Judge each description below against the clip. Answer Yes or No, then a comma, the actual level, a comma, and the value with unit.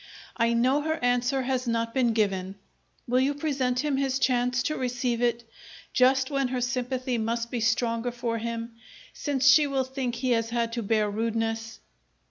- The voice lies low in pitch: No, high, 245 Hz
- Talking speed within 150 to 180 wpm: Yes, average, 175 wpm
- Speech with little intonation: Yes, narrow, 2.2 semitones